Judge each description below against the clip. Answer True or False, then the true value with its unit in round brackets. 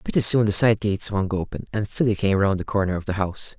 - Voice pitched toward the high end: False (100 Hz)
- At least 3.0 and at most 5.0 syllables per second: False (6.2 syllables/s)